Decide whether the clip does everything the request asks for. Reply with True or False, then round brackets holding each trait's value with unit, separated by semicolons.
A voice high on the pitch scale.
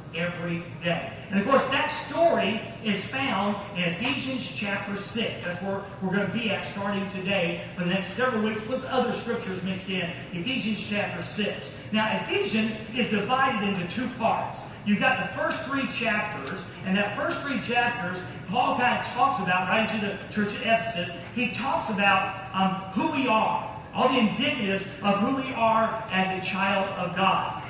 True (205 Hz)